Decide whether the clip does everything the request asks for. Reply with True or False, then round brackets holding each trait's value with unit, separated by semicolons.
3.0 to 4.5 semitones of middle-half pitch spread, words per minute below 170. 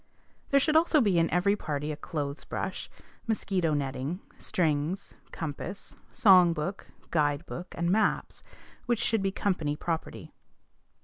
False (4.9 semitones; 140 wpm)